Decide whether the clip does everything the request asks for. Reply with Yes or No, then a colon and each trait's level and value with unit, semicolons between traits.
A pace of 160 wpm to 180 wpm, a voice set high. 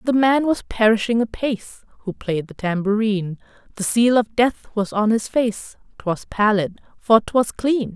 Yes: average, 165 wpm; high, 220 Hz